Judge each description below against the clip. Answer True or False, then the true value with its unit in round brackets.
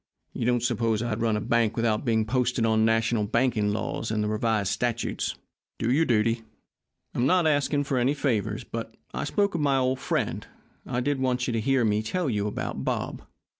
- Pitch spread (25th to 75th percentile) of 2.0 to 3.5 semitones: True (3.1 semitones)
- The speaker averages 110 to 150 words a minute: False (190 wpm)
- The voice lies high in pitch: False (115 Hz)